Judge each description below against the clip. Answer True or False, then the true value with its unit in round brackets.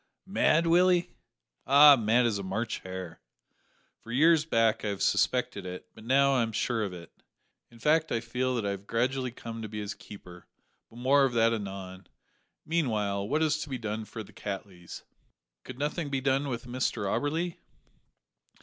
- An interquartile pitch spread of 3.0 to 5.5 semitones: True (5.1 semitones)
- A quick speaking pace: False (180 wpm)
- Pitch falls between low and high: False (120 Hz)